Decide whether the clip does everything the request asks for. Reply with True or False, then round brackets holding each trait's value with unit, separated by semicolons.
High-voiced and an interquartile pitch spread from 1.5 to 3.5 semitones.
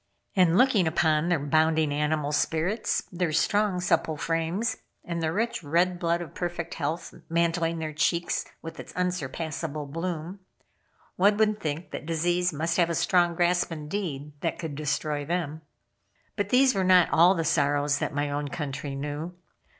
False (165 Hz; 2.9 semitones)